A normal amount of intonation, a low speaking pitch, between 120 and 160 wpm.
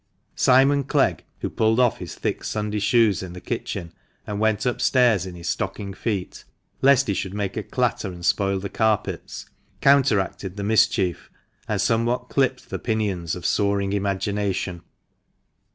Yes: average, 3.5 semitones; low, 105 Hz; average, 155 wpm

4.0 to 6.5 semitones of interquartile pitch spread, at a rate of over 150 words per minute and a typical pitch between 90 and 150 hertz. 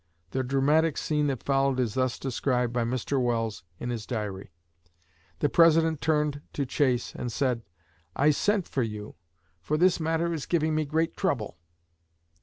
Yes: average, 4.3 semitones; average, 160 wpm; low, 135 Hz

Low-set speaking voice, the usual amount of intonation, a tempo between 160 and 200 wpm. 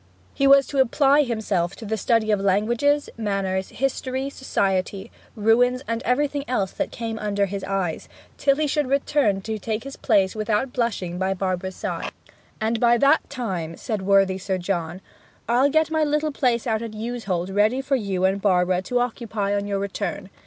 No: high, 220 Hz; average, 4.7 semitones; average, 180 wpm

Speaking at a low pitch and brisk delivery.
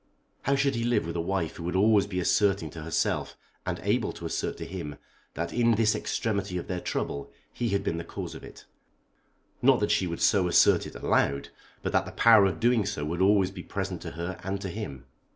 Yes: very low, 95 Hz; fast, 225 wpm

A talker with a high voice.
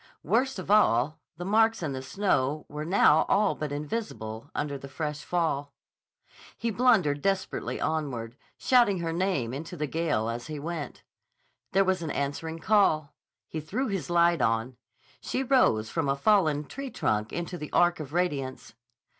No: medium, 160 Hz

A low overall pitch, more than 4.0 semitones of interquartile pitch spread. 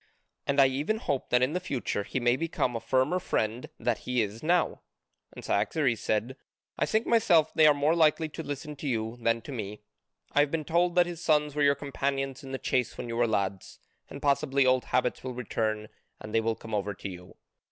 Yes: low, 130 Hz; average, 4.7 semitones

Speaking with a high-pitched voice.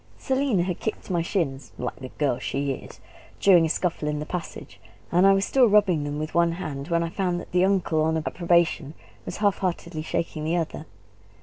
No: medium, 170 Hz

